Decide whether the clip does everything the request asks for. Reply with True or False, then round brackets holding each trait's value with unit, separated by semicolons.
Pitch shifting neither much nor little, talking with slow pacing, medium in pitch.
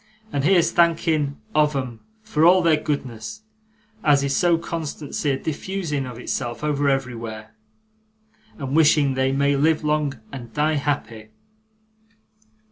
True (3.0 semitones; 130 wpm; 145 Hz)